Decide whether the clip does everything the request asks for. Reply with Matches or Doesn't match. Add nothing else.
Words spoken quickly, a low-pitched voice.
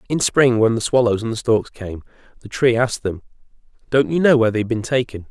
Matches